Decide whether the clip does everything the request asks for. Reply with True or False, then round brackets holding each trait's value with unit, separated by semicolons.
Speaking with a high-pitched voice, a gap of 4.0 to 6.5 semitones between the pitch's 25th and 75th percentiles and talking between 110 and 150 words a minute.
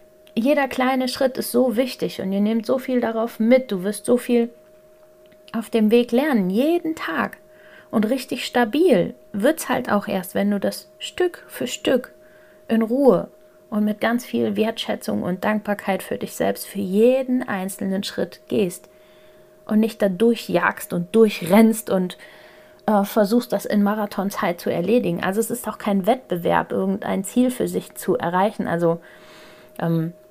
False (225 Hz; 4.3 semitones; 160 wpm)